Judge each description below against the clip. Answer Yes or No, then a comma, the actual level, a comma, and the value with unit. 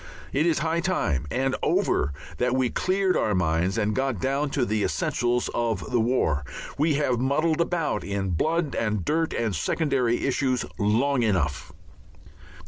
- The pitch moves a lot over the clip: Yes, wide, 5.9 semitones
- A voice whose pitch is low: Yes, low, 125 Hz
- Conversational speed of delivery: Yes, average, 155 wpm